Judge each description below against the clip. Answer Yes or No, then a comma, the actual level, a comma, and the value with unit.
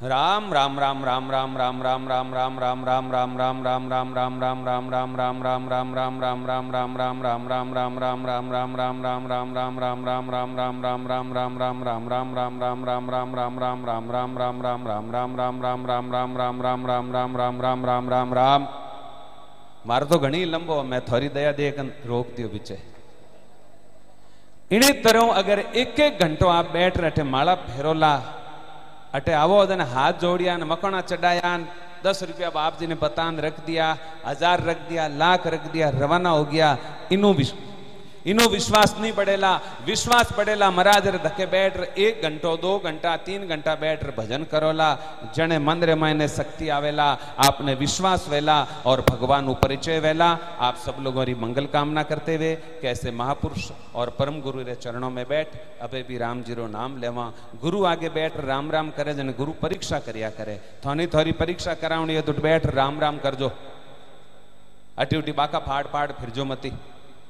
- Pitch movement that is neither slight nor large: Yes, average, 4.3 semitones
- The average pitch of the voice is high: No, medium, 140 Hz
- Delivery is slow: No, average, 160 wpm